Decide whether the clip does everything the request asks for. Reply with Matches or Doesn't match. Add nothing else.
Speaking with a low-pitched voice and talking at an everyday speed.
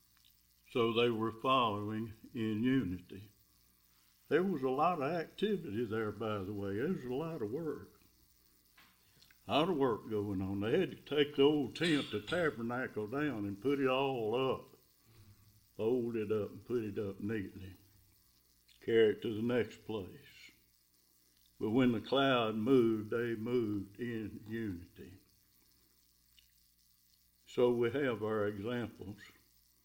Matches